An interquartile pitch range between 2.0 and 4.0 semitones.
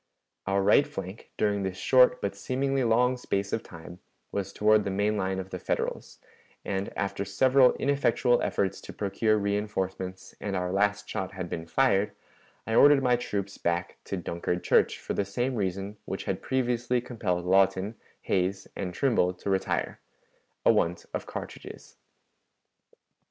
Yes: average, 3.7 semitones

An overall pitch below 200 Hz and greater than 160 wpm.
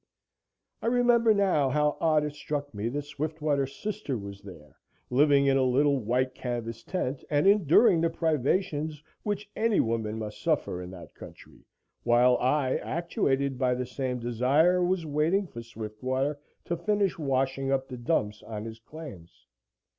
No: medium, 140 Hz; average, 155 wpm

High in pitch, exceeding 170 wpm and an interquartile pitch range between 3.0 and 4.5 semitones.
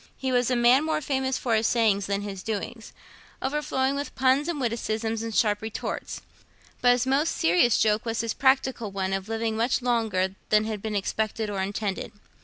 Yes: high, 225 Hz; average, 190 wpm; average, 3.6 semitones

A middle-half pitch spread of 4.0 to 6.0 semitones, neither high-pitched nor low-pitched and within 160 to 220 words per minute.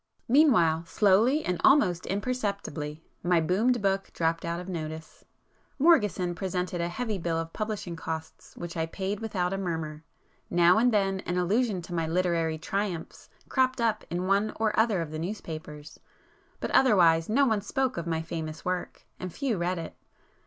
Yes: average, 4.4 semitones; medium, 180 Hz; average, 165 wpm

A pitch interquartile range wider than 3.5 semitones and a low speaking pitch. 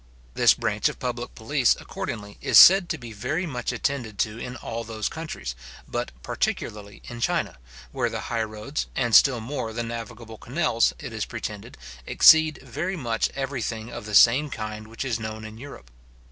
Yes: average, 4.0 semitones; low, 115 Hz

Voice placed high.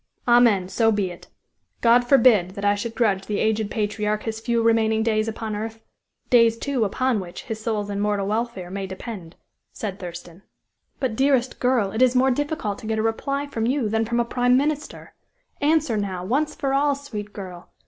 Yes: high, 225 Hz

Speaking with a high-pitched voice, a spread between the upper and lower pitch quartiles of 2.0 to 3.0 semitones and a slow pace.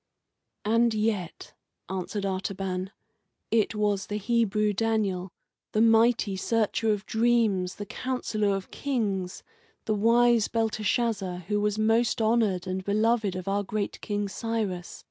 Yes: high, 210 Hz; narrow, 2.6 semitones; slow, 125 wpm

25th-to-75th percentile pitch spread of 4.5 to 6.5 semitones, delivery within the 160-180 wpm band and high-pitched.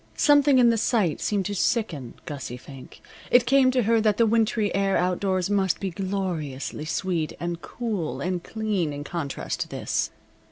Yes: average, 5.0 semitones; average, 170 wpm; high, 195 Hz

